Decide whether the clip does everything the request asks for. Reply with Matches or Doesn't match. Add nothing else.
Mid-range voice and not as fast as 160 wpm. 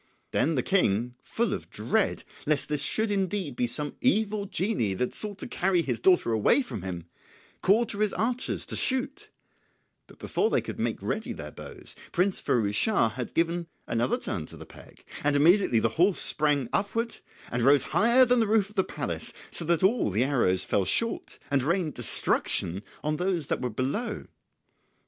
Doesn't match